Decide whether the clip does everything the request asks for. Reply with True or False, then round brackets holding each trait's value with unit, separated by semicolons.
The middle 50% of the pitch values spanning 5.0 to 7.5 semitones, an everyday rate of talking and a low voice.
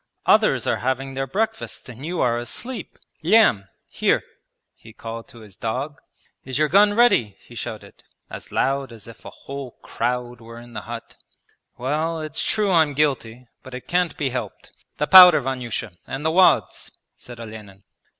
True (5.3 semitones; 170 wpm; 130 Hz)